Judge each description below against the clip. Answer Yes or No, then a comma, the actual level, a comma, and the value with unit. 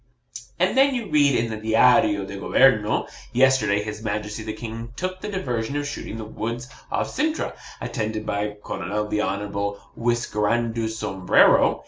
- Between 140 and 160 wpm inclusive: Yes, average, 150 wpm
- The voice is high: No, low, 110 Hz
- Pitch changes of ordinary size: Yes, average, 3.5 semitones